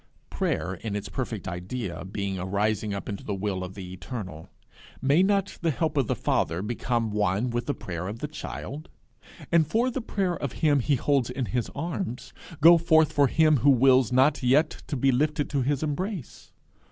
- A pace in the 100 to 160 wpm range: No, average, 195 wpm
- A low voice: Yes, low, 125 Hz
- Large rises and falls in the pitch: Yes, wide, 6.8 semitones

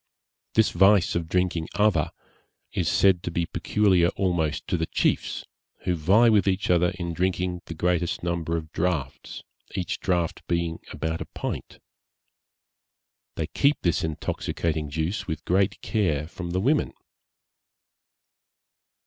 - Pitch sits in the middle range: No, very low, 85 Hz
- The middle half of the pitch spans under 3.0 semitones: Yes, narrow, 2.5 semitones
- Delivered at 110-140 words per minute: Yes, slow, 135 wpm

